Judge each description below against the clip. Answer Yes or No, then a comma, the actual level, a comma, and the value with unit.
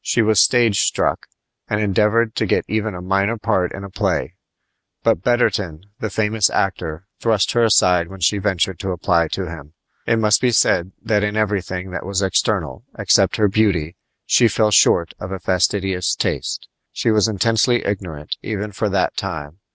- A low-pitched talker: Yes, low, 100 Hz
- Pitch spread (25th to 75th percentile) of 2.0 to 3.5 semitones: Yes, average, 3.1 semitones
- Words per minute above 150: Yes, average, 175 wpm